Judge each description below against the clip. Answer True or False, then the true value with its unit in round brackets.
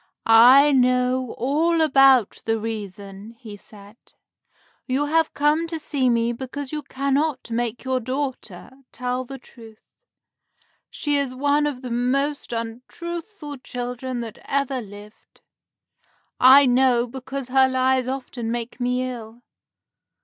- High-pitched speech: True (255 Hz)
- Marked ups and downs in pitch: False (2.8 semitones)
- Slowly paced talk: True (130 wpm)